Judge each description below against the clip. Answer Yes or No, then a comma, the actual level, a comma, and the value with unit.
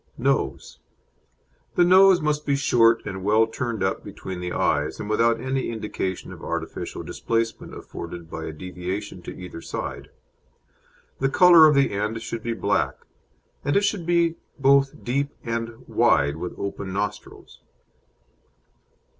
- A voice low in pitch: Yes, low, 115 Hz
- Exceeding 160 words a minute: No, average, 145 wpm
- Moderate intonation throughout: No, wide, 6.6 semitones